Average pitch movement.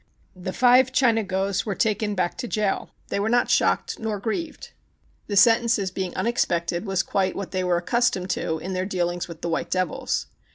Yes: average, 3.6 semitones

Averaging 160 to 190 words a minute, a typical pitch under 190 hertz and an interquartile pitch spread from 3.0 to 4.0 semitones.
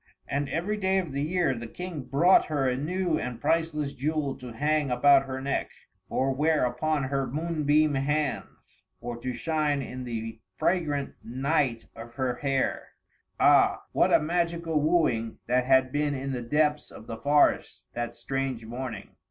Yes: average, 165 wpm; medium, 140 Hz; average, 3.4 semitones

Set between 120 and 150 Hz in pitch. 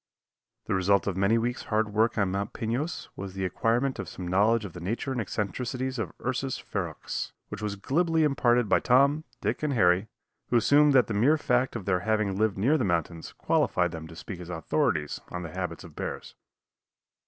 No: low, 110 Hz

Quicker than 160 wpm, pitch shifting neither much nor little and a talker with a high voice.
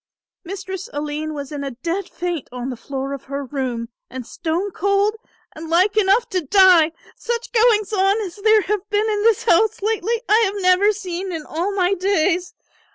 Yes: average, 185 wpm; average, 4.9 semitones; very high, 370 Hz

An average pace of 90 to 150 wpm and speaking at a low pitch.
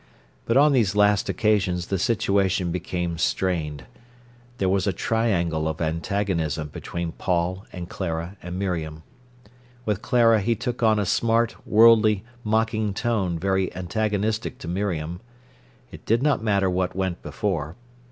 Yes: average, 140 wpm; very low, 95 Hz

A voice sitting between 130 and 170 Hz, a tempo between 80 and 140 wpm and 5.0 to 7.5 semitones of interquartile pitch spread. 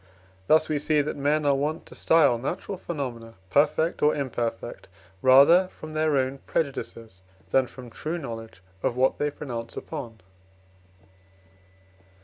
No: medium, 140 Hz; slow, 135 wpm; average, 4.5 semitones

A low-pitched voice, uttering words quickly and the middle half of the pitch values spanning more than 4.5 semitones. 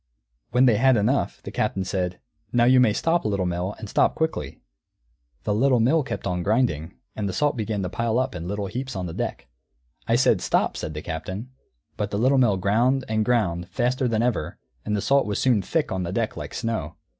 Yes: low, 110 Hz; fast, 215 wpm; average, 5.1 semitones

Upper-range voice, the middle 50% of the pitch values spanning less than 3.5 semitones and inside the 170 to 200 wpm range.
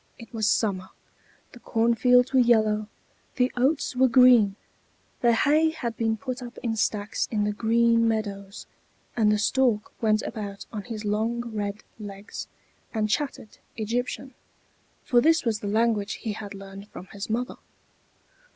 No: high, 225 Hz; average, 2.7 semitones; average, 150 wpm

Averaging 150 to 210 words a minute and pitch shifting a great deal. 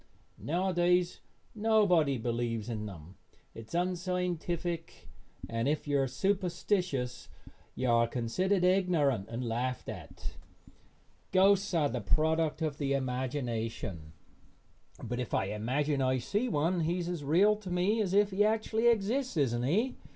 No: average, 140 wpm; wide, 6.9 semitones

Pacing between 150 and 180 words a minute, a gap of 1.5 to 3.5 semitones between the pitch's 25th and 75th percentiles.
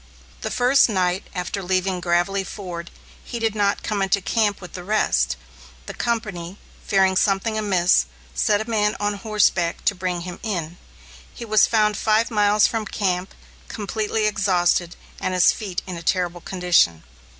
Yes: average, 160 wpm; average, 3.0 semitones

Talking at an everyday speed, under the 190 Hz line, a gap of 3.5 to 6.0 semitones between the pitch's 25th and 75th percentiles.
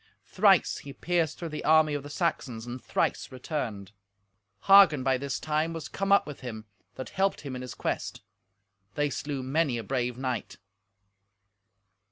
Yes: average, 165 wpm; medium, 140 Hz; average, 3.8 semitones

